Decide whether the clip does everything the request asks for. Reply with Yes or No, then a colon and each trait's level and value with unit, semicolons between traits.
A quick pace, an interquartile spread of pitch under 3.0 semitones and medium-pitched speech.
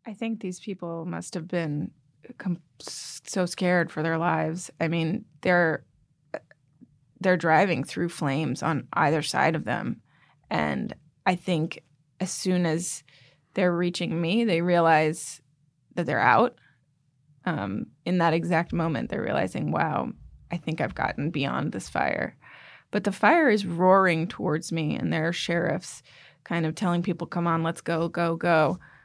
No: average, 155 wpm; narrow, 2.4 semitones; medium, 165 Hz